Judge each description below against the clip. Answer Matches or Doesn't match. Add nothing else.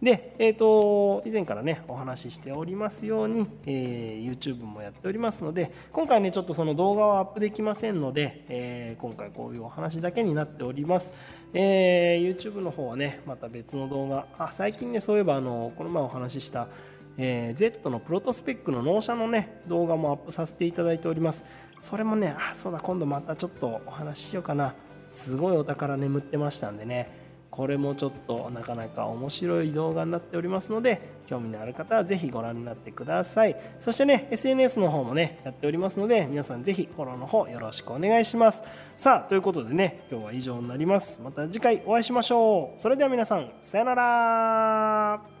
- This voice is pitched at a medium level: Matches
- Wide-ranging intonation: Matches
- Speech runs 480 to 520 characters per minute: Doesn't match